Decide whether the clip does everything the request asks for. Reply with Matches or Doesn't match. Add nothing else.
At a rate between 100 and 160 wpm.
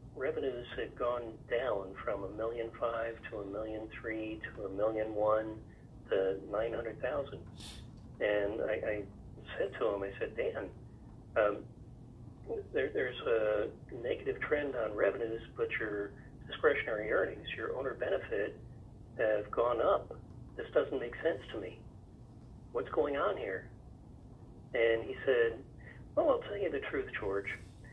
Matches